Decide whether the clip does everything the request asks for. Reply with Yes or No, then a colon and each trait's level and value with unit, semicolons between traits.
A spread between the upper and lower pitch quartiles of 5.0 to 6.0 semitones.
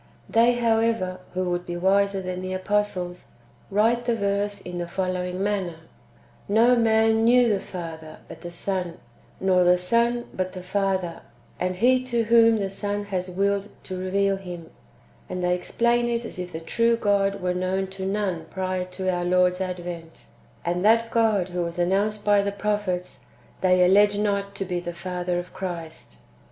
No: narrow, 2.5 semitones